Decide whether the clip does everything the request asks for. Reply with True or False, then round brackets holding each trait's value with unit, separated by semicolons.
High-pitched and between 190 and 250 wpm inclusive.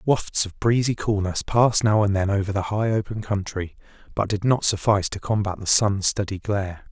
False (105 Hz; 200 wpm)